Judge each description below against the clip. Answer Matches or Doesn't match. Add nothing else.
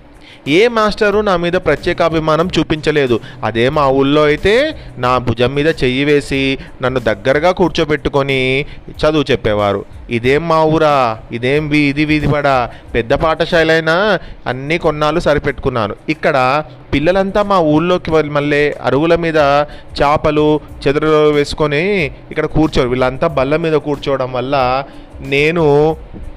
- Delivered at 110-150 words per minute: Matches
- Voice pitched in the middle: Matches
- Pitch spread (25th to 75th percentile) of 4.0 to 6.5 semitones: Doesn't match